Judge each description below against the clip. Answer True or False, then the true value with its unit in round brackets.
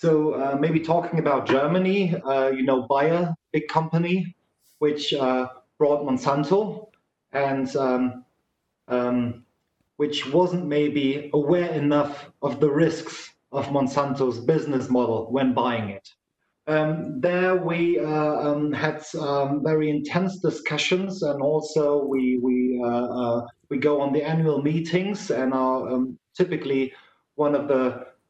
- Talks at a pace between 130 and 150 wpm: True (135 wpm)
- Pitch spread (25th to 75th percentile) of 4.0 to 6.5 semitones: False (3.4 semitones)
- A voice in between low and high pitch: True (145 Hz)